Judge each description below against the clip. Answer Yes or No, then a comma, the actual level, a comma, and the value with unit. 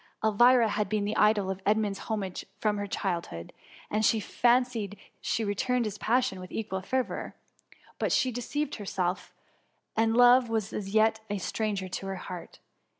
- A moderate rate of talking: Yes, average, 165 wpm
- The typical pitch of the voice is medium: No, high, 215 Hz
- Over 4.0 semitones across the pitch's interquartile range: No, average, 2.9 semitones